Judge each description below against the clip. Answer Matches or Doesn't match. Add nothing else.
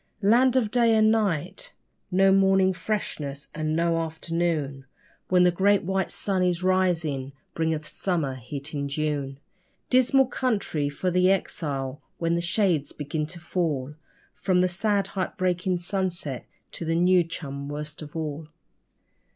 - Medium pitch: Matches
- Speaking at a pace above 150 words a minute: Doesn't match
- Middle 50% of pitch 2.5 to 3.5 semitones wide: Doesn't match